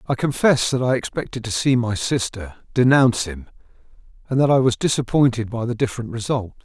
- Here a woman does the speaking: No, male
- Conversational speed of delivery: Yes, average, 180 wpm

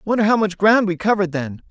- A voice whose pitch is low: No, high, 195 Hz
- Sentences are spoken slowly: No, fast, 245 wpm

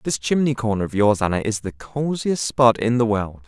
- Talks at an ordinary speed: No, fast, 225 wpm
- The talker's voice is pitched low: Yes, low, 115 Hz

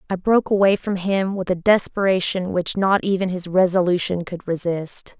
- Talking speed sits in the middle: Yes, average, 175 wpm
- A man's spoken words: No, female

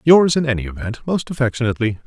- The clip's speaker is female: No, male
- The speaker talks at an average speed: Yes, average, 175 wpm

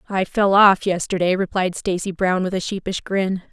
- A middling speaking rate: Yes, average, 190 wpm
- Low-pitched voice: No, high, 190 Hz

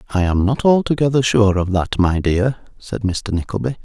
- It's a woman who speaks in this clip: No, male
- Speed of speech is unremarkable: Yes, average, 190 wpm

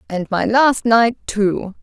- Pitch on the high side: Yes, high, 220 Hz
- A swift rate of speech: No, average, 165 wpm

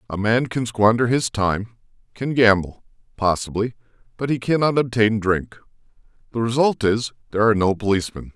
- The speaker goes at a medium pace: Yes, average, 150 wpm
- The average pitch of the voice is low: Yes, low, 110 Hz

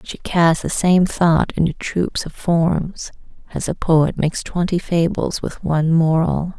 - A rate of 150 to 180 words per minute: Yes, average, 165 wpm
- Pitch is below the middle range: No, medium, 170 Hz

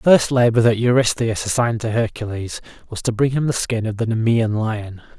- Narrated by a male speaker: Yes, male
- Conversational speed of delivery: No, fast, 210 wpm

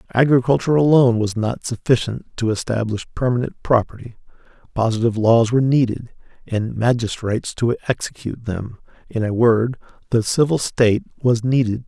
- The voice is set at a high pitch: No, low, 120 Hz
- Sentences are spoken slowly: Yes, slow, 130 wpm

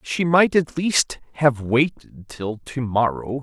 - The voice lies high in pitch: No, low, 130 Hz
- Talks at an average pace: Yes, average, 160 wpm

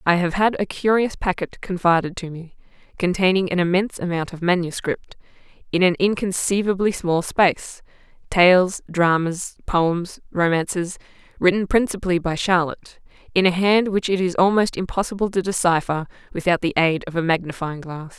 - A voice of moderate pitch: Yes, medium, 180 Hz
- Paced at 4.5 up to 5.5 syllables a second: Yes, 5.1 syllables/s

